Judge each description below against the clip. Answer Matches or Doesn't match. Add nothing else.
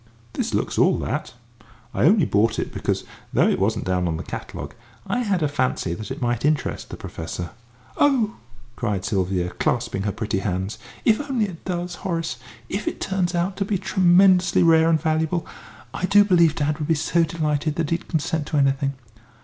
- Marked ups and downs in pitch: Matches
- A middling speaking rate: Matches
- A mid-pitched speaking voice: Matches